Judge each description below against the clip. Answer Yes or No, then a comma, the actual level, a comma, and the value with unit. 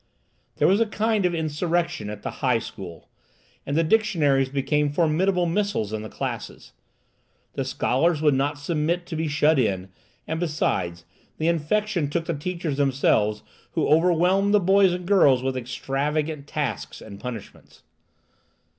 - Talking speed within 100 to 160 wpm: Yes, average, 150 wpm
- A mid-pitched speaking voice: Yes, medium, 155 Hz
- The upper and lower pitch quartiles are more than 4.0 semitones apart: Yes, average, 4.6 semitones